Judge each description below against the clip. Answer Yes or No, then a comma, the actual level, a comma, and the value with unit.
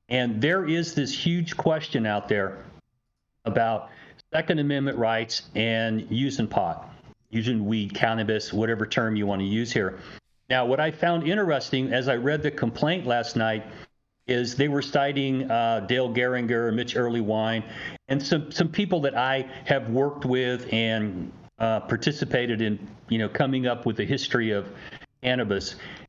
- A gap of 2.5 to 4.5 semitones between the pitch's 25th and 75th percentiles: Yes, average, 3.8 semitones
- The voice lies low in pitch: Yes, low, 120 Hz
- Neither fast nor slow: Yes, average, 155 wpm